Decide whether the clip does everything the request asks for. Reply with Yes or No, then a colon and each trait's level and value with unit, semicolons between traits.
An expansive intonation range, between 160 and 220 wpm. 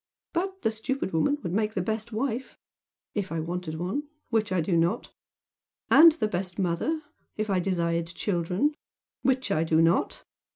Yes: wide, 5.8 semitones; average, 165 wpm